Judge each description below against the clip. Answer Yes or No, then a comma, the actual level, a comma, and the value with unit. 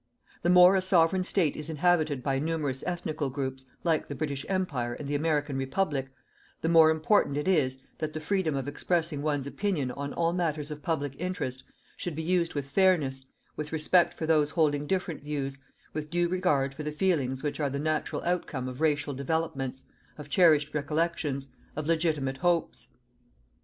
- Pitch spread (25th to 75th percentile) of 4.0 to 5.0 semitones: No, average, 3.3 semitones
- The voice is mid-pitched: Yes, medium, 150 Hz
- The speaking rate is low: No, average, 175 wpm